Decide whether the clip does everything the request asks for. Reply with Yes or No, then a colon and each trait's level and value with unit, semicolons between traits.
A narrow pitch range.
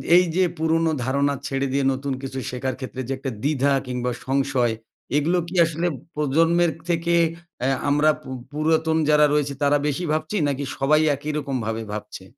No: average, 3.1 semitones